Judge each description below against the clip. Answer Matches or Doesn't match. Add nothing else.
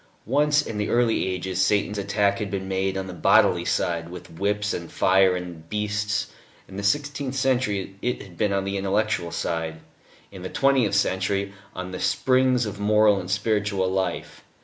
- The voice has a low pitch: Matches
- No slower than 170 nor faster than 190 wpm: Matches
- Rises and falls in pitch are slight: Matches